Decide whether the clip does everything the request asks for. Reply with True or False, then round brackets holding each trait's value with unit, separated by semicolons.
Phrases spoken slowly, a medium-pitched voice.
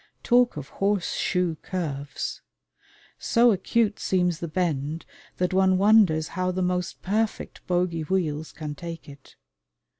True (130 wpm; 180 Hz)